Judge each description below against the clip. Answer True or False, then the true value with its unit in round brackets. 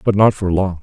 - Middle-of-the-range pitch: False (95 Hz)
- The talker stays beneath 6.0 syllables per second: True (5.5 syllables/s)